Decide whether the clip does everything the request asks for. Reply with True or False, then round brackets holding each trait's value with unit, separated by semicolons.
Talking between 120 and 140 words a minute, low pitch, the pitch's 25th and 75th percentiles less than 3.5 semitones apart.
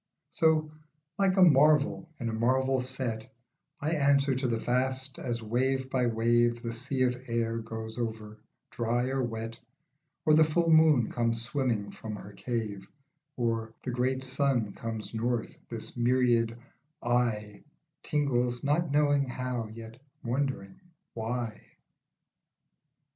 True (135 wpm; 120 Hz; 2.9 semitones)